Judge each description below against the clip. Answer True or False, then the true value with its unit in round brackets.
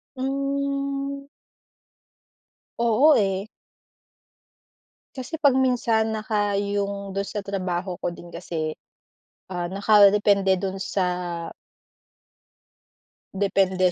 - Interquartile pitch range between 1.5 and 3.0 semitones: False (4.8 semitones)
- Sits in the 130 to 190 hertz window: False (200 Hz)